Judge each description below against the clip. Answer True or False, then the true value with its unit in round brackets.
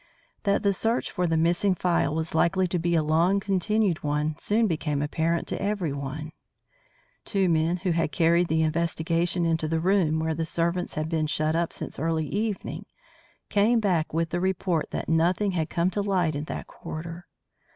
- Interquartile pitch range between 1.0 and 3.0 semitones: True (2.7 semitones)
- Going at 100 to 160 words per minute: False (180 wpm)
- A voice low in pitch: False (170 Hz)